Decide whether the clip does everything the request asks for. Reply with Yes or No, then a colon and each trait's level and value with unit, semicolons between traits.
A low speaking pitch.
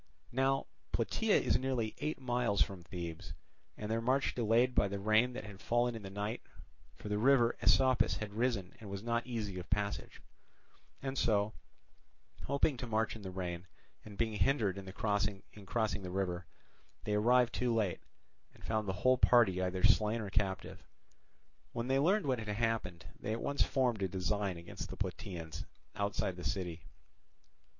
Yes: low, 105 Hz